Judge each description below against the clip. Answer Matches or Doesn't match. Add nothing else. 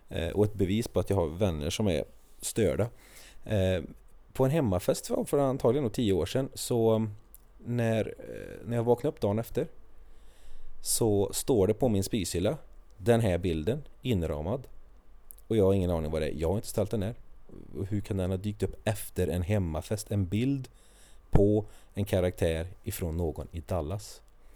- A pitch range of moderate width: Matches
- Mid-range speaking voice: Doesn't match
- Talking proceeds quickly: Doesn't match